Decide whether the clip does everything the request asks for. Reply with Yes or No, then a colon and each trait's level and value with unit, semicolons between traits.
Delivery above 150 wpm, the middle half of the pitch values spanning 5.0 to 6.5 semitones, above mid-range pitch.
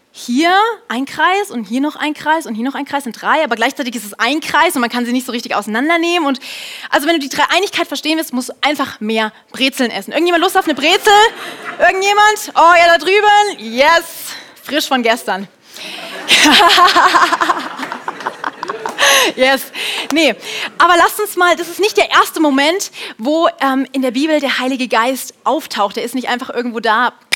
Yes: average, 185 wpm; wide, 5.4 semitones; very high, 295 Hz